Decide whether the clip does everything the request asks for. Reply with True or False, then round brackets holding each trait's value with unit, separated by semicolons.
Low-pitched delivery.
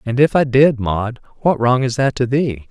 True (125 Hz)